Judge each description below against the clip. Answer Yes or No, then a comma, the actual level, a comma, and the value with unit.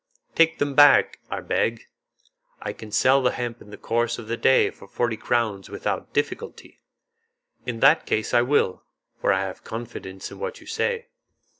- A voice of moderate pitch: No, low, 120 Hz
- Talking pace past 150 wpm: Yes, average, 175 wpm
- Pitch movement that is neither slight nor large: Yes, average, 3.6 semitones